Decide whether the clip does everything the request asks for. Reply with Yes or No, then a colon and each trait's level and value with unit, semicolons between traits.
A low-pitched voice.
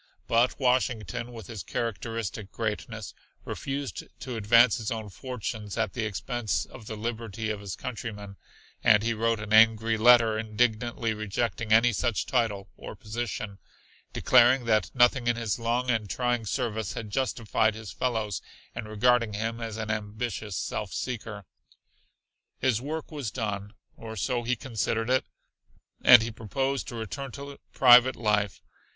Yes: low, 115 Hz